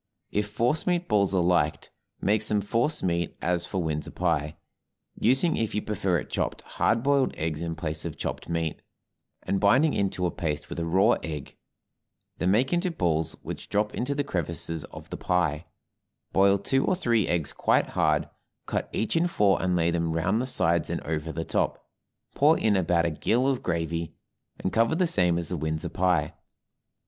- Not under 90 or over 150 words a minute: No, average, 190 wpm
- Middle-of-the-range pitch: No, very low, 90 Hz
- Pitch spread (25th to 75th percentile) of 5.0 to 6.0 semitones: Yes, wide, 5.5 semitones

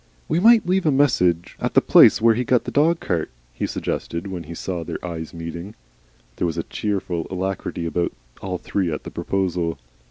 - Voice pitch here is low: Yes, very low, 90 Hz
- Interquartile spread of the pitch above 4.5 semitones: Yes, wide, 5.4 semitones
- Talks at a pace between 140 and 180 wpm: No, average, 195 wpm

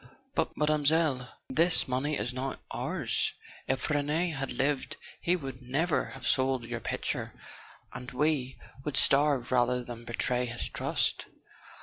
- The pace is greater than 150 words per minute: No, average, 140 wpm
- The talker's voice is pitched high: No, low, 135 Hz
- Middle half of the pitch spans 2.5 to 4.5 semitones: Yes, average, 3.1 semitones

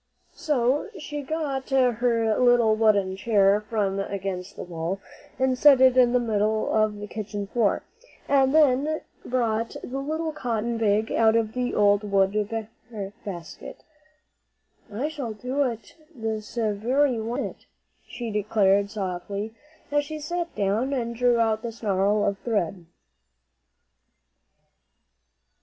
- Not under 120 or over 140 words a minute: Yes, slow, 135 wpm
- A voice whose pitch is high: Yes, high, 225 Hz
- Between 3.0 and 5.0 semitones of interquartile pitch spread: Yes, average, 3.9 semitones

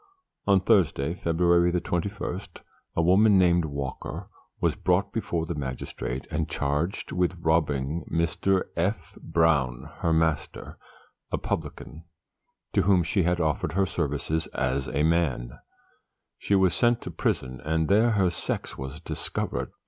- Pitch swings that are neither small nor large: Yes, average, 3.8 semitones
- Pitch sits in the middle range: No, very low, 85 Hz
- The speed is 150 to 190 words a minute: No, slow, 135 wpm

